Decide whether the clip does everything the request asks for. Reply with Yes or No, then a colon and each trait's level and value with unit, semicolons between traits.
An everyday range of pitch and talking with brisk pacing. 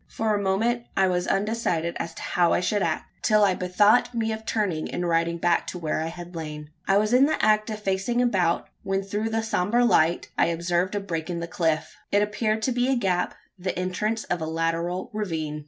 Yes: average, 4.1 semitones; fast, 220 wpm